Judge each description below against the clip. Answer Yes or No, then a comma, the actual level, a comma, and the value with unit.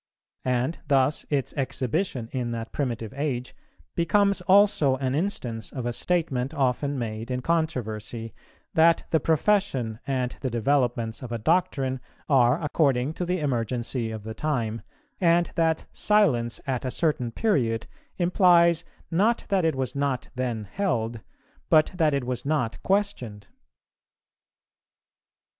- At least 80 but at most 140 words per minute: Yes, slow, 135 wpm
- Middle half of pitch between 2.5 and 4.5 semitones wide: No, wide, 5.6 semitones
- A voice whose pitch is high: No, low, 135 Hz